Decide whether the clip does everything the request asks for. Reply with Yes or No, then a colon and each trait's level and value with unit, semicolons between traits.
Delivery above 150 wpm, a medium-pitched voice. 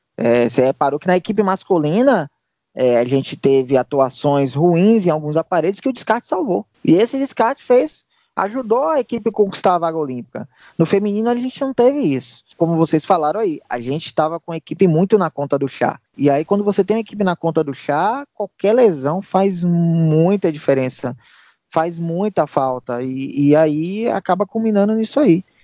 Yes: fast, 185 wpm; medium, 170 Hz